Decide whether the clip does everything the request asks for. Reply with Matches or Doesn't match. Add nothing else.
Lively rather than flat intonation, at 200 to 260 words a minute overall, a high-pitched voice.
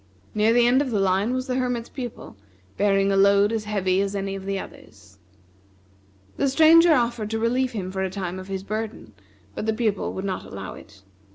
Doesn't match